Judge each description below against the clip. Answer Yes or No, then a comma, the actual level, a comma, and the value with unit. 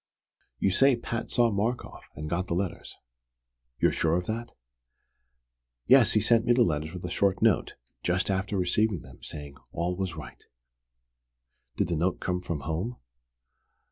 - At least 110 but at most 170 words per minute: Yes, average, 160 wpm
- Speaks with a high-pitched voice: No, very low, 95 Hz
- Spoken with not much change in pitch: No, average, 4.7 semitones